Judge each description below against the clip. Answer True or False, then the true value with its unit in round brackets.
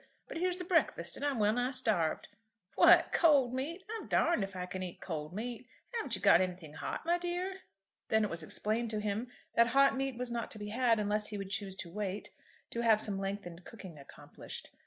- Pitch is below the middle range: False (220 Hz)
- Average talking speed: False (215 wpm)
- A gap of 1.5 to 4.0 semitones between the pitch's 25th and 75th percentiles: False (5.5 semitones)